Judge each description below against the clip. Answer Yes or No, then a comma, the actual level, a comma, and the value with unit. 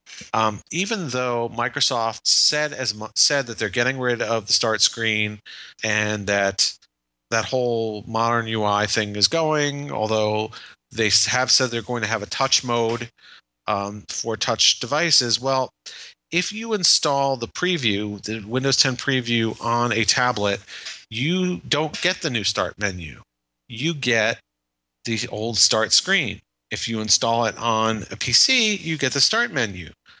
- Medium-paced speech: Yes, average, 155 wpm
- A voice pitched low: Yes, low, 115 Hz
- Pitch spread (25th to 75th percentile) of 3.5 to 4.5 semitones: Yes, average, 4.0 semitones